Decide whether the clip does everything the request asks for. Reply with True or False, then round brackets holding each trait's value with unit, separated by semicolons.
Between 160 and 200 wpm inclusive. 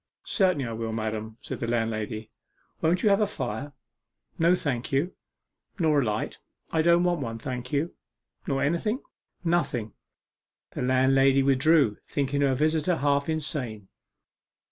False (145 wpm)